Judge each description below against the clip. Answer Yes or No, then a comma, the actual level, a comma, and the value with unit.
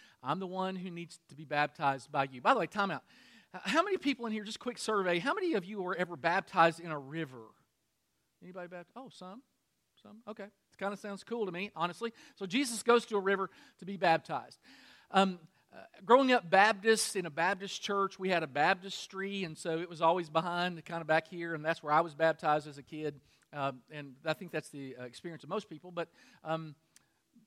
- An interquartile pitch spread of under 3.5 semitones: No, average, 4.1 semitones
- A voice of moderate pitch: Yes, medium, 180 Hz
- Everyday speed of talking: No, fast, 225 wpm